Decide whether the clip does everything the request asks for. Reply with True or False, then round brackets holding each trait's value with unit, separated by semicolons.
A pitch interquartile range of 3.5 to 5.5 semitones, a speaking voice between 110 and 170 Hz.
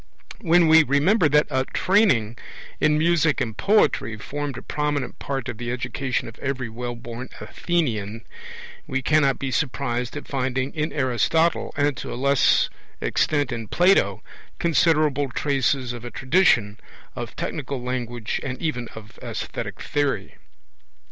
True (3.8 semitones; 135 Hz)